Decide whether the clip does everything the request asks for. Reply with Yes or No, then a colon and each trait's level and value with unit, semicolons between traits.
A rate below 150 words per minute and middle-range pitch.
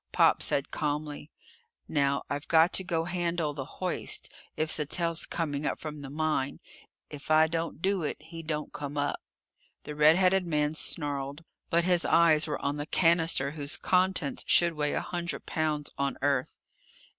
No: average, 170 wpm; medium, 155 Hz